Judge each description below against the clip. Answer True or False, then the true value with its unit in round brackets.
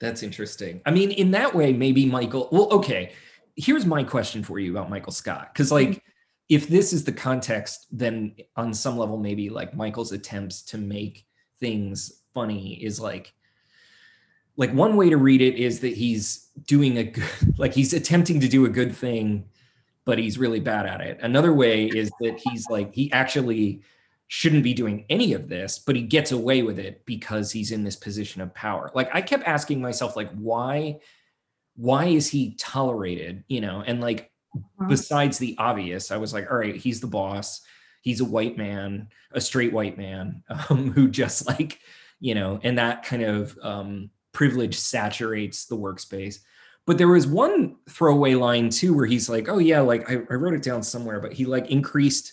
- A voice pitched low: True (120 Hz)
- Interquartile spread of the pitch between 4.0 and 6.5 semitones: True (4.7 semitones)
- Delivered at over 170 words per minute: True (190 wpm)